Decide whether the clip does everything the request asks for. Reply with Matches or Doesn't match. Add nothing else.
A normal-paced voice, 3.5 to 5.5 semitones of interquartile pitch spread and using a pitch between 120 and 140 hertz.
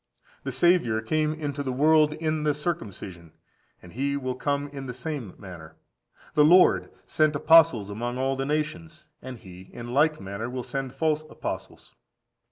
Matches